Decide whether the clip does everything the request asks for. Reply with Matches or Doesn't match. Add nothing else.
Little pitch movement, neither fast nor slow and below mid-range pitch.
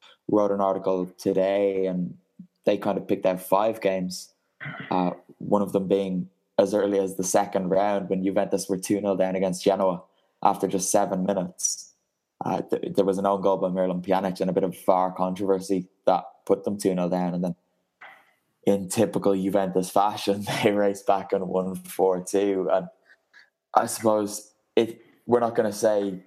Matches